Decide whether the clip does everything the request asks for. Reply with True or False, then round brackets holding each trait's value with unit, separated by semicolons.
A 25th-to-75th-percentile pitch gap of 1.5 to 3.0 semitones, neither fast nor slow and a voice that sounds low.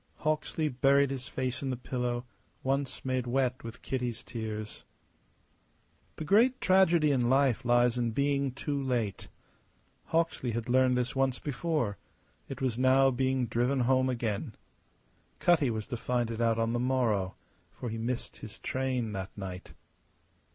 True (2.5 semitones; 150 wpm; 125 Hz)